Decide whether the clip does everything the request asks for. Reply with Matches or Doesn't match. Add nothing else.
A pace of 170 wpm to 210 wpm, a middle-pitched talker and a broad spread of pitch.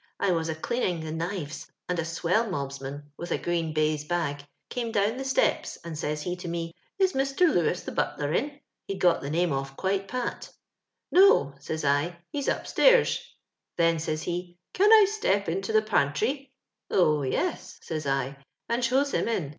Matches